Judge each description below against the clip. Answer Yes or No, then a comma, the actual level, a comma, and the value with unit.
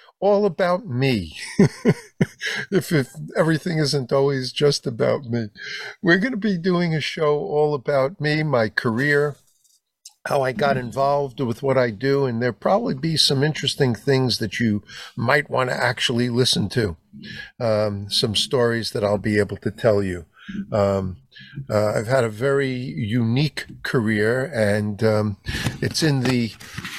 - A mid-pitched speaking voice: No, low, 130 Hz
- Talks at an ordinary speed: Yes, average, 155 wpm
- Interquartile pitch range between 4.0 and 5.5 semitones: Yes, average, 4.9 semitones